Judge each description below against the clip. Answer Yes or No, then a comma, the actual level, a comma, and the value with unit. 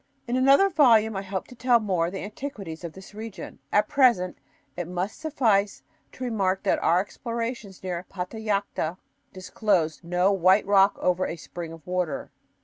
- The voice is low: No, high, 195 Hz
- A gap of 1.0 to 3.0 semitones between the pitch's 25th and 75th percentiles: No, average, 4.0 semitones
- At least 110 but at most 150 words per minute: No, average, 165 wpm